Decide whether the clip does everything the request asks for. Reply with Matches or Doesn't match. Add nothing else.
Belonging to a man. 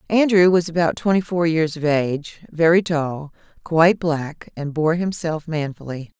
Doesn't match